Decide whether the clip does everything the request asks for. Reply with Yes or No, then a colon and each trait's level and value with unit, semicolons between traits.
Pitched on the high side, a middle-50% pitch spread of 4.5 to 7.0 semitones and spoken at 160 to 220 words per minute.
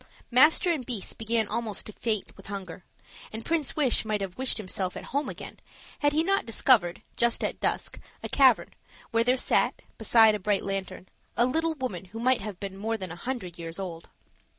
Yes: high, 220 Hz; average, 4.8 semitones; average, 195 wpm